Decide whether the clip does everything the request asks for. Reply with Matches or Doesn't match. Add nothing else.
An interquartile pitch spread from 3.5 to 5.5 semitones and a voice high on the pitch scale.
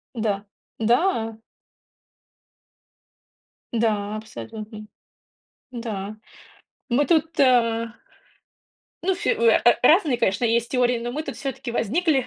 Matches